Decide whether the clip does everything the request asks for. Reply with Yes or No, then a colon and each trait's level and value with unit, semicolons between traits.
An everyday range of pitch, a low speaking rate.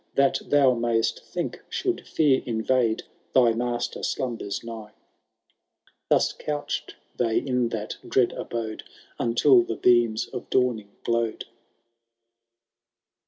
No: narrow, 2.0 semitones; slow, 110 wpm